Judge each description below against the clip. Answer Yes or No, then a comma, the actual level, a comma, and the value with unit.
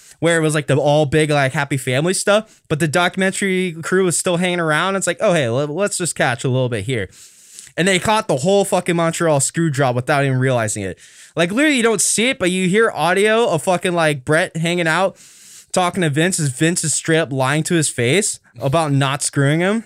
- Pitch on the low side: No, medium, 165 Hz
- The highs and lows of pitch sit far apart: No, average, 4.2 semitones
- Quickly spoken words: Yes, fast, 225 wpm